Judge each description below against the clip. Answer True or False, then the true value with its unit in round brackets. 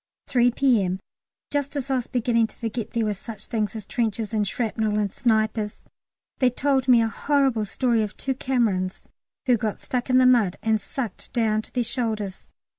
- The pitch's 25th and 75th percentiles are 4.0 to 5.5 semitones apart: False (3.0 semitones)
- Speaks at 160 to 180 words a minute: False (190 wpm)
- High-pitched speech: True (230 Hz)